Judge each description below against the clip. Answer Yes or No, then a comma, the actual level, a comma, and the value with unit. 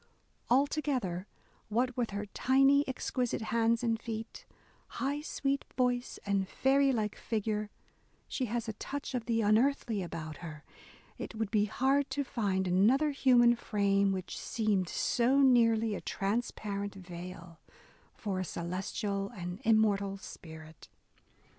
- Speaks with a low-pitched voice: No, high, 220 Hz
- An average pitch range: Yes, average, 4.2 semitones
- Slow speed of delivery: Yes, slow, 130 wpm